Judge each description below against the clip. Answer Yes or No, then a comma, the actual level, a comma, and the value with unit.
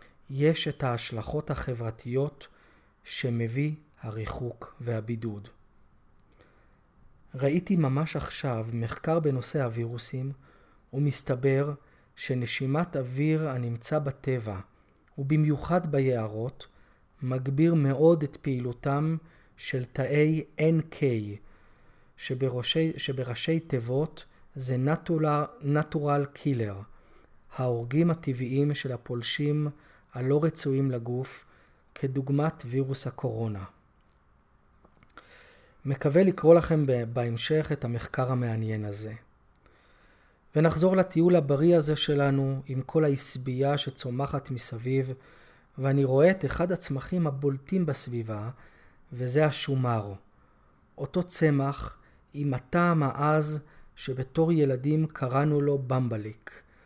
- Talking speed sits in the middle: No, slow, 85 wpm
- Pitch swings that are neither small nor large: Yes, average, 3.5 semitones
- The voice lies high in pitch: No, low, 135 Hz